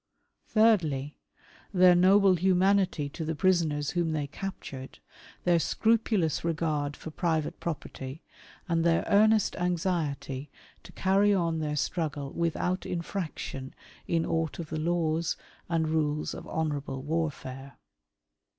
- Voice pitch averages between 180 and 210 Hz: No, medium, 165 Hz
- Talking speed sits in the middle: No, slow, 120 wpm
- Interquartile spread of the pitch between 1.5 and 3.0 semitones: No, average, 3.4 semitones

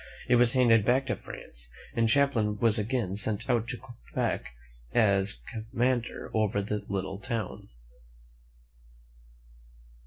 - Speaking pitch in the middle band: No, low, 115 Hz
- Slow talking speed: Yes, slow, 120 wpm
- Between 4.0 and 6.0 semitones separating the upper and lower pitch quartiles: No, average, 3.1 semitones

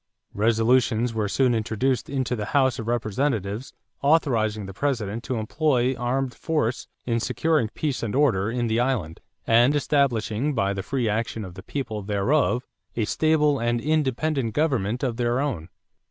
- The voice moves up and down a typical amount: Yes, average, 3.8 semitones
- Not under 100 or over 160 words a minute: Yes, average, 155 wpm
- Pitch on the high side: No, low, 120 Hz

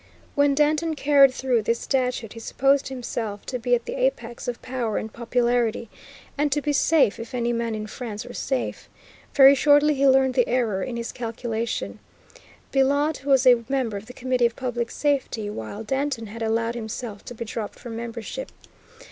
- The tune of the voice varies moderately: Yes, average, 3.1 semitones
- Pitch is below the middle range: No, high, 245 Hz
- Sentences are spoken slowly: No, average, 180 wpm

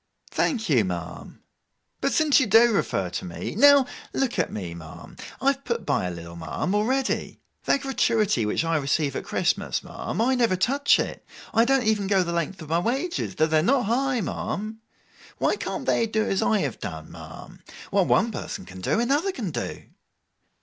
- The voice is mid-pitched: No, high, 210 Hz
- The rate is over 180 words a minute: Yes, average, 190 wpm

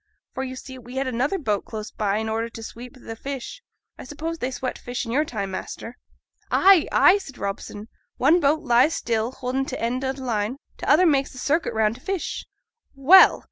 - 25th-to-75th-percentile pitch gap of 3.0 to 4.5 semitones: Yes, average, 3.7 semitones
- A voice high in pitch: Yes, very high, 255 Hz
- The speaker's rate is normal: No, fast, 210 wpm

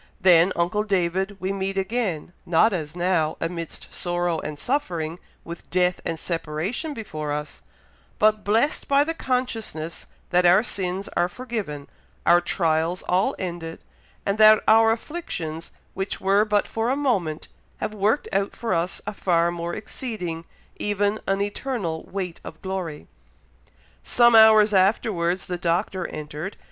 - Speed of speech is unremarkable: Yes, average, 145 wpm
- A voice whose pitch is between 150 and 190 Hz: Yes, medium, 185 Hz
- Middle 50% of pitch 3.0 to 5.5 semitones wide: Yes, average, 4.1 semitones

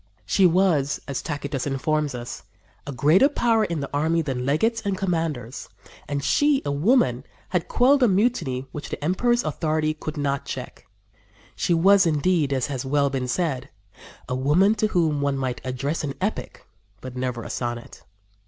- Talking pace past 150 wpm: Yes, average, 170 wpm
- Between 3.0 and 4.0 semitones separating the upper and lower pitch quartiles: No, average, 5.3 semitones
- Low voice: No, medium, 150 Hz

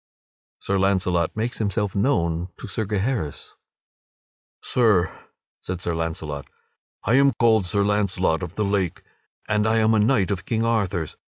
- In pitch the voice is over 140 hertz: No, low, 100 Hz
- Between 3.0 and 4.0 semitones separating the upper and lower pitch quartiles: Yes, average, 3.7 semitones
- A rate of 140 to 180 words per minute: Yes, average, 155 wpm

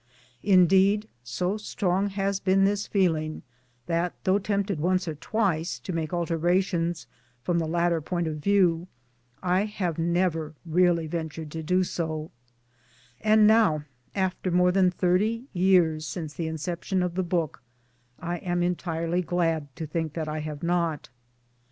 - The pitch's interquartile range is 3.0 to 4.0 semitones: No, narrow, 2.6 semitones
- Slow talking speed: No, average, 145 wpm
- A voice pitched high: No, medium, 175 Hz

